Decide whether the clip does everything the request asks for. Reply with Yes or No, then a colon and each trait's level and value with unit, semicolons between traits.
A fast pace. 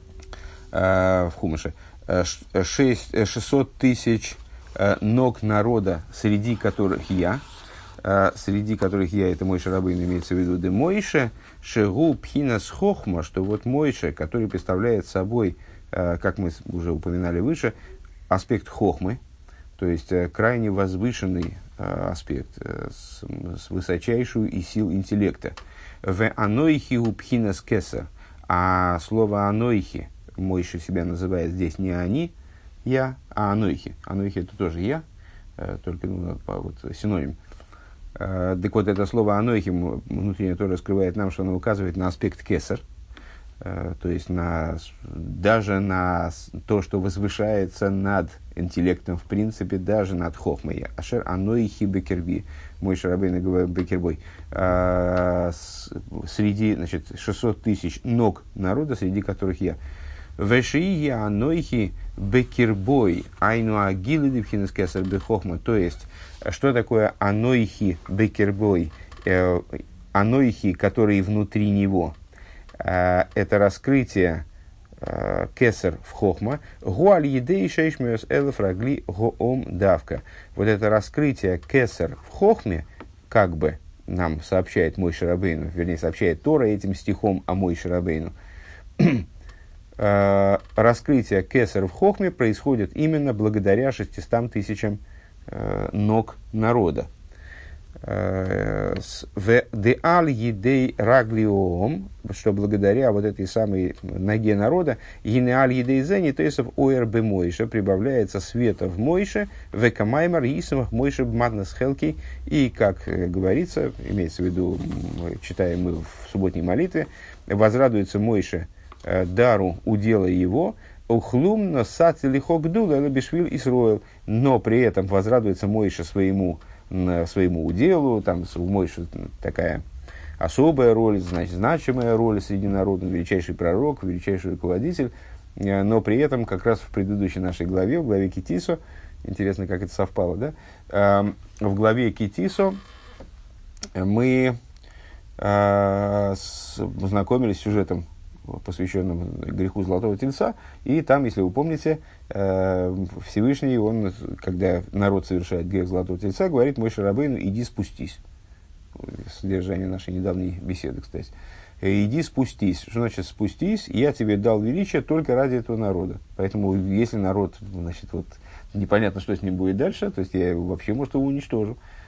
No: average, 115 wpm